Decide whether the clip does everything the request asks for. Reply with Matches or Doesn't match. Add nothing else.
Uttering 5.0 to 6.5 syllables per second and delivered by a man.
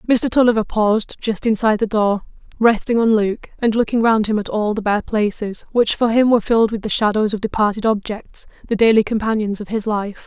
Doesn't match